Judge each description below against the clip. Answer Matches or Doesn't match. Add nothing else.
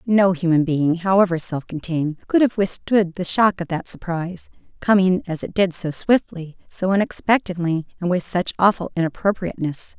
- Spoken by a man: Doesn't match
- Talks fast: Doesn't match